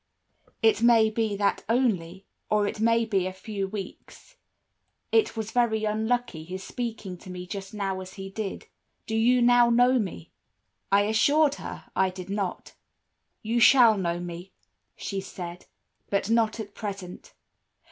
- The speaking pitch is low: No, high, 210 Hz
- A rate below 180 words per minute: Yes, average, 155 wpm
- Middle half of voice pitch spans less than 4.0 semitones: Yes, average, 3.3 semitones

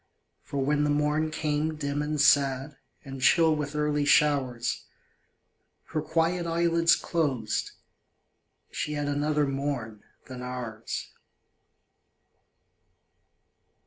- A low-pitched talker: No, medium, 145 Hz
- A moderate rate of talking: No, slow, 100 wpm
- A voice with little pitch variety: Yes, narrow, 2.1 semitones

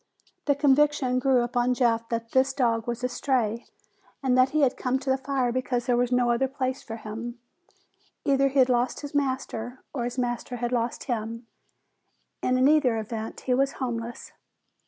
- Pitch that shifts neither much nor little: No, narrow, 2.0 semitones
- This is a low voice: No, very high, 250 Hz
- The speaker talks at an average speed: Yes, average, 180 wpm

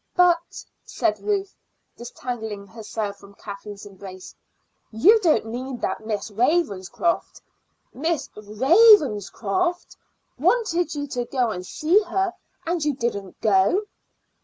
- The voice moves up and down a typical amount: No, wide, 8.8 semitones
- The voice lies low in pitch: No, high, 245 Hz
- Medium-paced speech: No, slow, 110 wpm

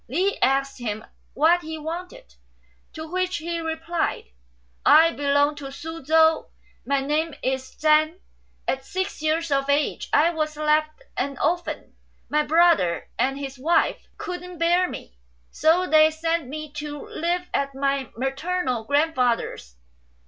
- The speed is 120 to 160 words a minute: Yes, average, 140 wpm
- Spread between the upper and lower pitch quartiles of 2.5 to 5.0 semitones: Yes, average, 3.3 semitones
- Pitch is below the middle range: No, very high, 310 Hz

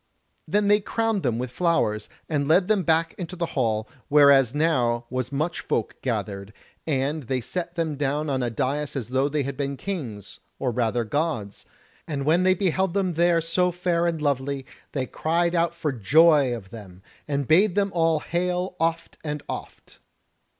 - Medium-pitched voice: Yes, medium, 150 Hz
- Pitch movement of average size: Yes, average, 5.0 semitones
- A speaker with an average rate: Yes, average, 175 wpm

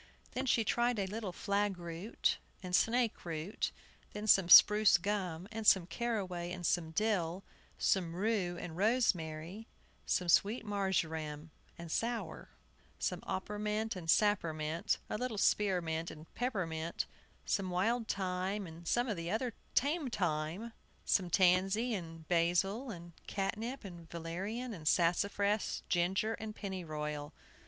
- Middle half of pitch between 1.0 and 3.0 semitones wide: No, average, 4.2 semitones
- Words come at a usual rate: No, slow, 130 wpm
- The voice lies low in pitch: No, high, 190 Hz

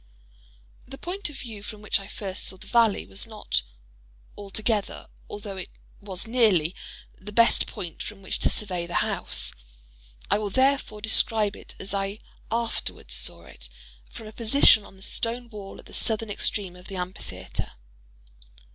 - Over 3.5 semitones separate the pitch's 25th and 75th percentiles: No, average, 3.0 semitones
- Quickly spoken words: No, average, 160 wpm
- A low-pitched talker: No, high, 205 Hz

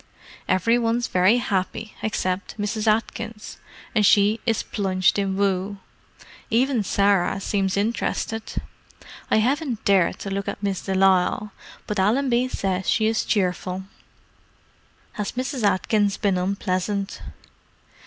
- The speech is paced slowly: Yes, slow, 125 wpm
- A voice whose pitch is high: Yes, high, 205 Hz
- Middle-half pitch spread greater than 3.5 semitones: No, average, 2.7 semitones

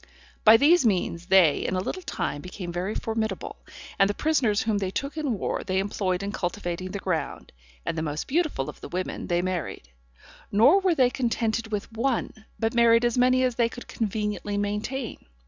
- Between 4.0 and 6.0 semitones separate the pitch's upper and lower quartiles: Yes, average, 4.7 semitones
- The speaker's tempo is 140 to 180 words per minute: No, average, 190 wpm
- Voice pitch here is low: No, high, 210 Hz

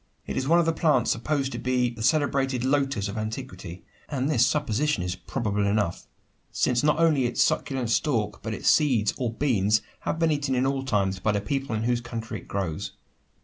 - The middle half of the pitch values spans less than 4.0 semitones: No, average, 4.5 semitones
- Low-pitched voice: Yes, low, 125 Hz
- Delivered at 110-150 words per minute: No, average, 200 wpm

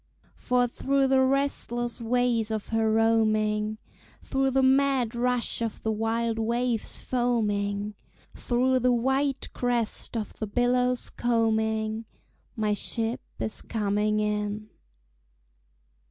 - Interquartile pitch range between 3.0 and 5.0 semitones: No, narrow, 2.4 semitones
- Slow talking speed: Yes, slow, 110 wpm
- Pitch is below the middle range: No, high, 230 Hz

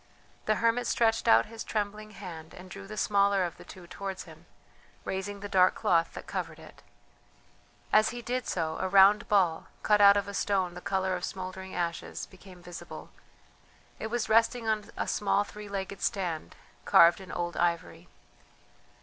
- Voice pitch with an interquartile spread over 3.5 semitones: No, average, 2.9 semitones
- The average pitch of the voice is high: Yes, high, 195 Hz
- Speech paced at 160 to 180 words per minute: Yes, average, 175 wpm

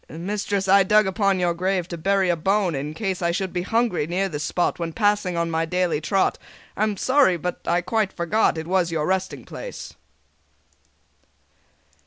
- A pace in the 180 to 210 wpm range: Yes, average, 185 wpm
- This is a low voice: No, medium, 185 Hz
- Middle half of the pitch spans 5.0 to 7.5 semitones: No, narrow, 2.6 semitones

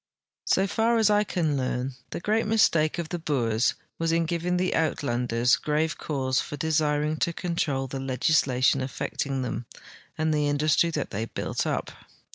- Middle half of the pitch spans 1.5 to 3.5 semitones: No, average, 4.1 semitones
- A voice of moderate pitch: Yes, medium, 150 Hz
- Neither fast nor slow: Yes, average, 165 wpm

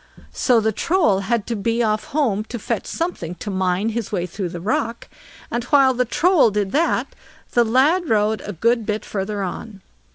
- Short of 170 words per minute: No, average, 190 wpm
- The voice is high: Yes, high, 220 Hz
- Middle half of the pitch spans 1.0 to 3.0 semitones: No, average, 3.7 semitones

